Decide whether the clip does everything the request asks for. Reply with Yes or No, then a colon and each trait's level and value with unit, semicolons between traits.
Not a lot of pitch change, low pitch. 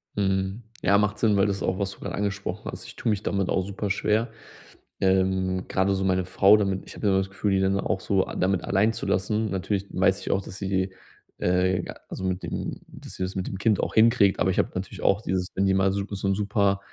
Yes: narrow, 1.2 semitones; very low, 95 Hz